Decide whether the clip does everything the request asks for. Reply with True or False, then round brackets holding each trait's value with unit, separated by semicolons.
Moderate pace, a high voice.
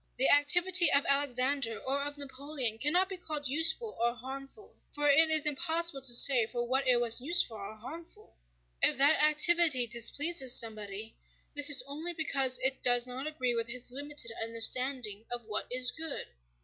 True (170 wpm; 275 Hz)